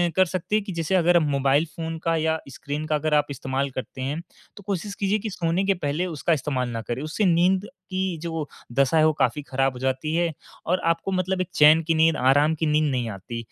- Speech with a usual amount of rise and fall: Yes, average, 4.1 semitones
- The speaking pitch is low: No, medium, 160 Hz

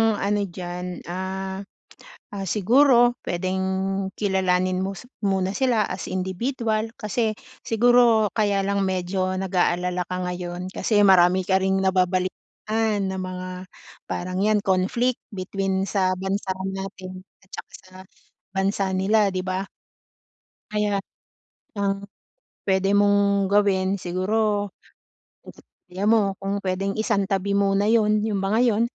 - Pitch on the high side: Yes, high, 195 Hz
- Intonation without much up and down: Yes, narrow, 1.9 semitones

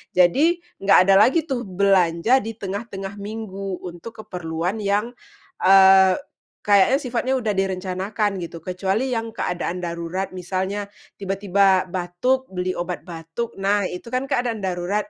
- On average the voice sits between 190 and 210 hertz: Yes, high, 195 Hz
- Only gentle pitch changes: No, average, 3.5 semitones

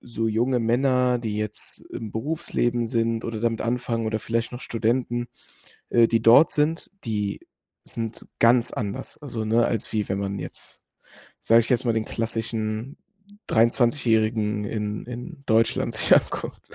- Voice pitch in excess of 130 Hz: No, low, 115 Hz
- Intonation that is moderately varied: No, narrow, 1.6 semitones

